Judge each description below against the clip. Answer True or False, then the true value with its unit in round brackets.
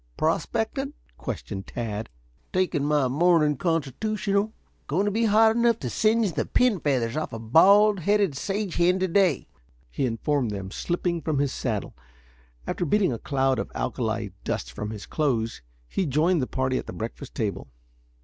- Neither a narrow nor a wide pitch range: False (8.0 semitones)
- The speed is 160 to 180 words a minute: True (165 wpm)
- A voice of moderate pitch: True (155 Hz)